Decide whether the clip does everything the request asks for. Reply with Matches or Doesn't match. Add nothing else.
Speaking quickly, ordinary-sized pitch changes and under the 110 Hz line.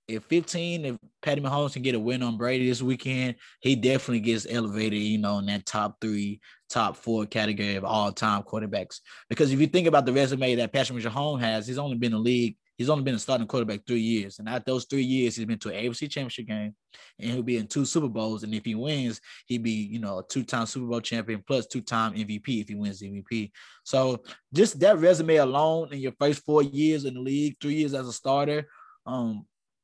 Doesn't match